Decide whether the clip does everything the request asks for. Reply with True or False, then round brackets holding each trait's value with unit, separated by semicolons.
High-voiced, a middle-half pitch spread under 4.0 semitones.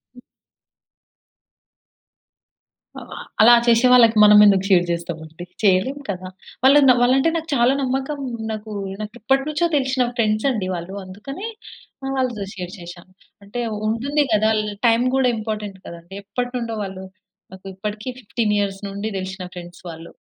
False (215 Hz; 4.7 semitones)